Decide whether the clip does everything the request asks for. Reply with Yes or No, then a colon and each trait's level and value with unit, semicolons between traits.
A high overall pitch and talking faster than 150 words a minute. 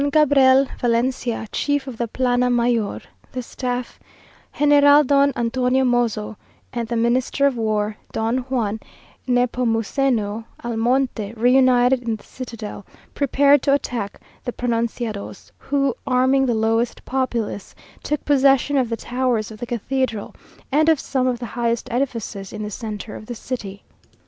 No: high, 245 Hz; average, 145 wpm